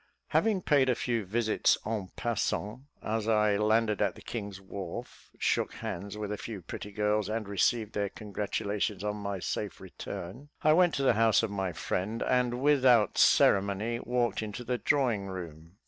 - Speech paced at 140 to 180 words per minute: Yes, average, 170 wpm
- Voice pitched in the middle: No, low, 105 Hz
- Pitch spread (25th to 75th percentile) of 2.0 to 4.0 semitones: Yes, average, 2.9 semitones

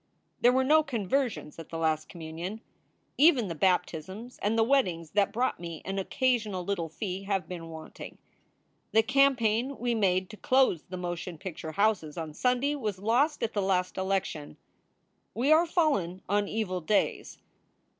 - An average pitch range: No, wide, 5.8 semitones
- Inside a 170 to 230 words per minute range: No, average, 160 wpm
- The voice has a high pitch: Yes, high, 200 Hz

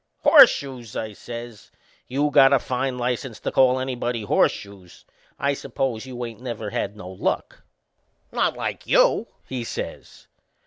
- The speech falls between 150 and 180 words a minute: No, average, 140 wpm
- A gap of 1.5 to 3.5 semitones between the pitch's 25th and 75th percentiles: Yes, average, 3.0 semitones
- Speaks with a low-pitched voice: Yes, low, 120 Hz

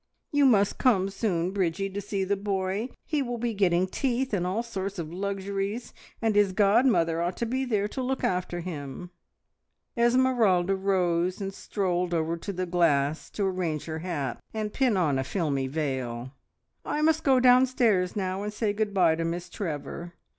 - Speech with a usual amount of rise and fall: Yes, average, 4.2 semitones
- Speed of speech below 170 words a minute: No, average, 175 wpm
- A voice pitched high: Yes, high, 195 Hz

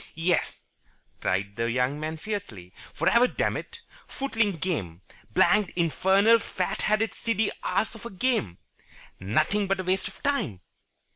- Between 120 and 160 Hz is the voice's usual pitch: No, medium, 185 Hz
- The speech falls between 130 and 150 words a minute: Yes, average, 140 wpm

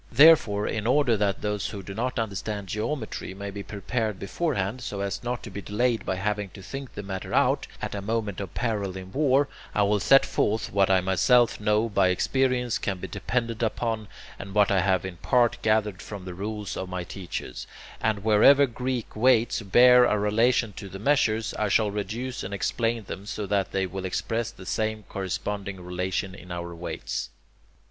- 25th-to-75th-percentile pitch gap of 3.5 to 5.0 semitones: No, average, 3.0 semitones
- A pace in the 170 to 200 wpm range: Yes, average, 190 wpm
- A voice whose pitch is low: Yes, low, 105 Hz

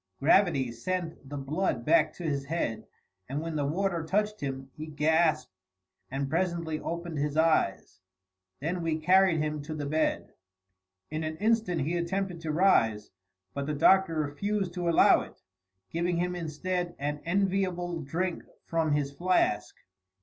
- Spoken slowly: No, average, 150 wpm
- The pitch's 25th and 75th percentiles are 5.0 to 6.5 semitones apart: No, average, 3.3 semitones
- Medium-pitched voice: Yes, medium, 160 Hz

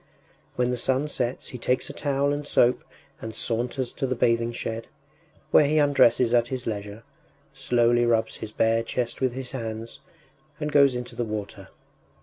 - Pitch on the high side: No, low, 120 Hz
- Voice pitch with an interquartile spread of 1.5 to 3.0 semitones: Yes, narrow, 2.6 semitones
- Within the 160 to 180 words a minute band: Yes, average, 170 wpm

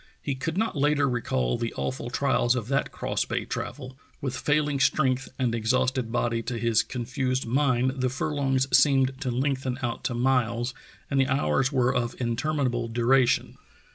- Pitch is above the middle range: No, low, 130 Hz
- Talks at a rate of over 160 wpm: Yes, average, 170 wpm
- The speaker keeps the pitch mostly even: Yes, narrow, 2.2 semitones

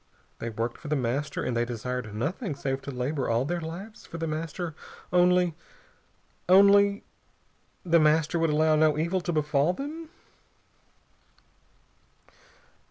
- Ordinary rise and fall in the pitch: Yes, average, 4.6 semitones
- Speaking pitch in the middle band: Yes, medium, 155 Hz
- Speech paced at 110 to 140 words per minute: Yes, slow, 135 wpm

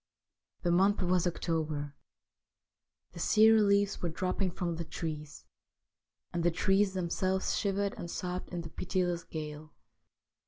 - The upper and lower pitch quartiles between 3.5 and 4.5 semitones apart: No, narrow, 2.6 semitones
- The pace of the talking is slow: Yes, slow, 130 wpm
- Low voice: No, medium, 175 Hz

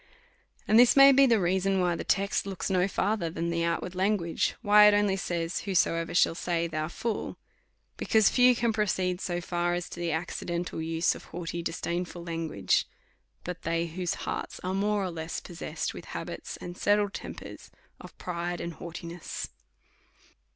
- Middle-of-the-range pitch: Yes, medium, 175 Hz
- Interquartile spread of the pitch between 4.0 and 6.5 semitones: No, average, 2.8 semitones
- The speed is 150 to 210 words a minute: Yes, average, 170 wpm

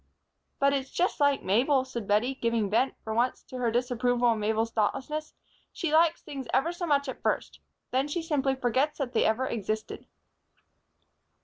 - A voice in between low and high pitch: No, very high, 260 Hz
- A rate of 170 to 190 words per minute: Yes, average, 175 wpm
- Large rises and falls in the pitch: No, average, 3.6 semitones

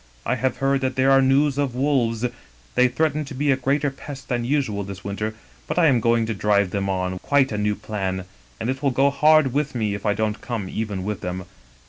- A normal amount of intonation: Yes, average, 4.9 semitones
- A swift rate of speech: Yes, fast, 235 wpm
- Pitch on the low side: Yes, low, 120 Hz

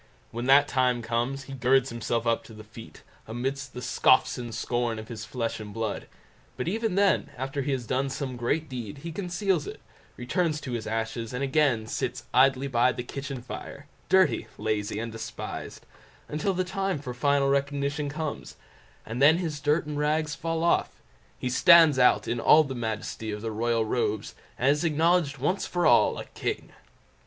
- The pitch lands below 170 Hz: Yes, low, 135 Hz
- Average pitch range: Yes, average, 4.3 semitones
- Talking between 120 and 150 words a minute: No, average, 180 wpm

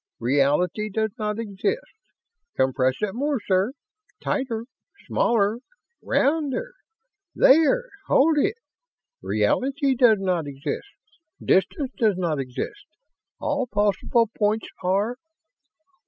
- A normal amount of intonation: No, wide, 6.6 semitones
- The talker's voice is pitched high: Yes, high, 220 Hz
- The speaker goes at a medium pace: No, slow, 95 wpm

